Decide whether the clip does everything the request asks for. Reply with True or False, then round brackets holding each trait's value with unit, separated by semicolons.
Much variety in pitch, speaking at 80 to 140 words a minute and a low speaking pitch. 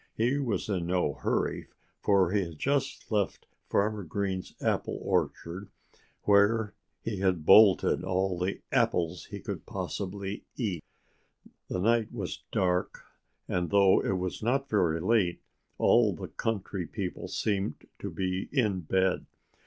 False (2.8 semitones; 135 wpm; 95 Hz)